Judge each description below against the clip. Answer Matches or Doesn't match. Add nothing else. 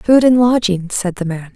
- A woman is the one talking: Matches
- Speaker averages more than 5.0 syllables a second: Doesn't match